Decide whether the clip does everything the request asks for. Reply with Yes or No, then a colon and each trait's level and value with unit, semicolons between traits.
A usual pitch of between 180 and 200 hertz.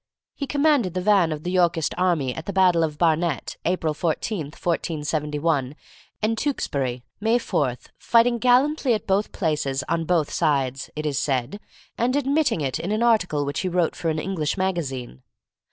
No: medium, 170 Hz